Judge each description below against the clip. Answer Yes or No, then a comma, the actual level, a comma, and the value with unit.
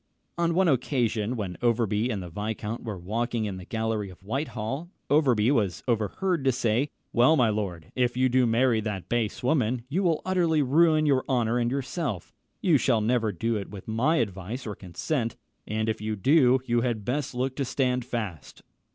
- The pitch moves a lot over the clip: No, average, 3.8 semitones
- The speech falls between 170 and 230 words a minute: Yes, average, 185 wpm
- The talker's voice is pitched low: Yes, low, 120 Hz